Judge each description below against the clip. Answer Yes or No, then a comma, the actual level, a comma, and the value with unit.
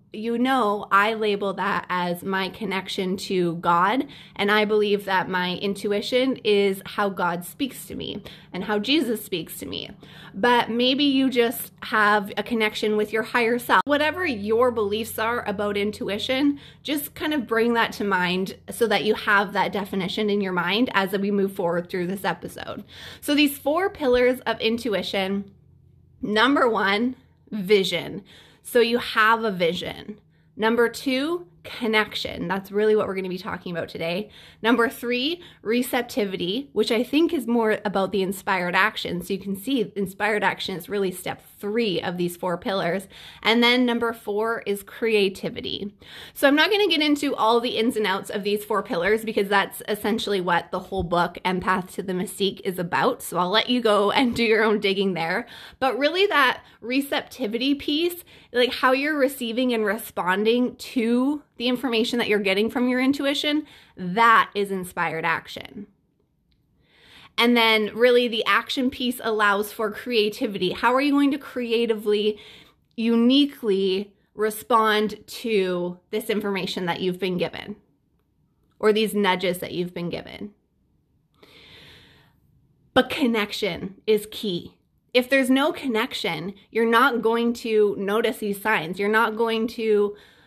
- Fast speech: No, average, 160 wpm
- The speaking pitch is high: Yes, high, 215 Hz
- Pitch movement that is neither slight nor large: Yes, average, 3.7 semitones